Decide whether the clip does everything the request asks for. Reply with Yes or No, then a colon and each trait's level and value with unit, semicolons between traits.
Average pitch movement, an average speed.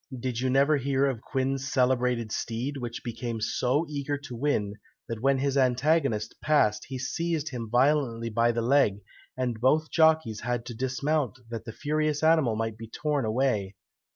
Yes: average, 3.7 semitones; average, 170 wpm